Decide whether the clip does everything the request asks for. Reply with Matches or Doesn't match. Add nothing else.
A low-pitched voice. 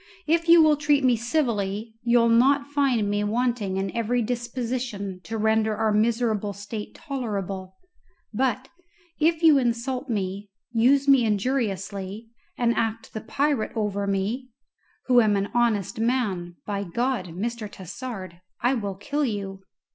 Doesn't match